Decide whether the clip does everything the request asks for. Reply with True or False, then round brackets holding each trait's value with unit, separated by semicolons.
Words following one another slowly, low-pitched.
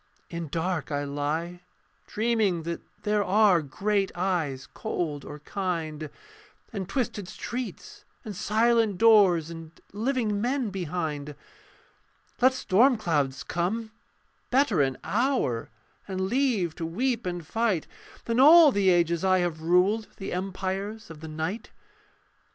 False (130 wpm; 185 Hz)